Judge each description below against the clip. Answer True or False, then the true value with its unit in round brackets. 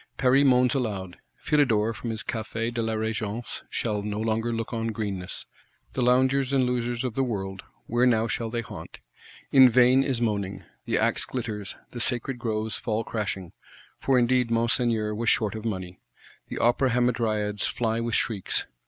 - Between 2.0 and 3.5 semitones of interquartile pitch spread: True (2.5 semitones)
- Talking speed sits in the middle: True (165 wpm)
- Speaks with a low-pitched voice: True (115 Hz)